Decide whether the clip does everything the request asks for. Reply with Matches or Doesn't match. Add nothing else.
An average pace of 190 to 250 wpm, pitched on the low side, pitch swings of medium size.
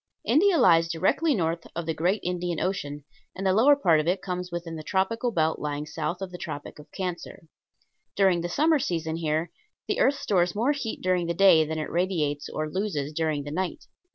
Doesn't match